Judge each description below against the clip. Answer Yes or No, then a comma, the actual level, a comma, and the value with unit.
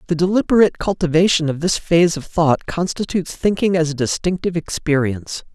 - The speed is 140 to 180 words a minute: Yes, average, 150 wpm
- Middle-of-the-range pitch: Yes, medium, 165 Hz